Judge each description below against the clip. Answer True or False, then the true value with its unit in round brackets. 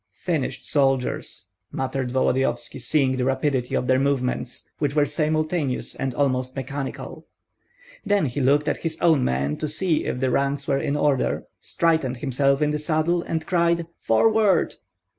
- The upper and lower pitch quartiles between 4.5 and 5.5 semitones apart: False (3.1 semitones)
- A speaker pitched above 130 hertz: True (140 Hz)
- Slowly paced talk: False (155 wpm)